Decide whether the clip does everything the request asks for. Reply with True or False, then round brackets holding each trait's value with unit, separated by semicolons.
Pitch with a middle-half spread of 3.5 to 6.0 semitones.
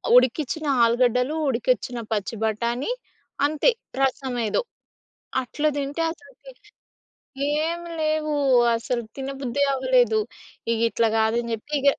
True (4.5 semitones)